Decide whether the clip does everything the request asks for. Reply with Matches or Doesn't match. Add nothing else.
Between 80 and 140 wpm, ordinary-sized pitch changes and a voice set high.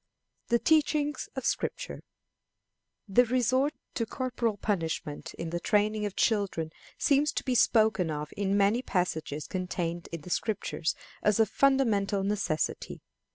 Doesn't match